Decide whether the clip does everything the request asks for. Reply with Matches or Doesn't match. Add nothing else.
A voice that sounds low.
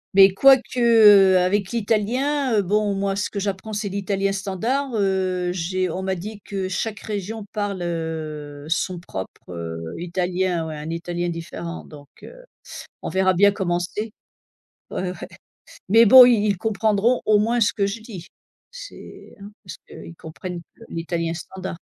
Doesn't match